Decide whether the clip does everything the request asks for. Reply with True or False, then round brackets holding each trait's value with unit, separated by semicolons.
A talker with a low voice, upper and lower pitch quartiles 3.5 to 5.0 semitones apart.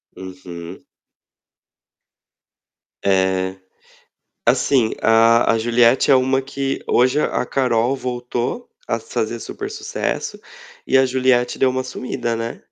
False (125 Hz; 2.7 semitones)